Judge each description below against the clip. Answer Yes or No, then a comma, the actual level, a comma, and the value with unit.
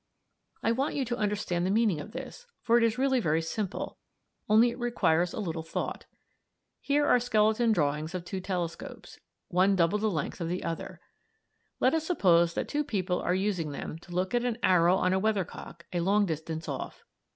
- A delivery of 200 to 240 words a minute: Yes, fast, 205 wpm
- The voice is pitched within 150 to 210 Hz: Yes, high, 190 Hz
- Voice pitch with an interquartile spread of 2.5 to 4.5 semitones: No, average, 5.3 semitones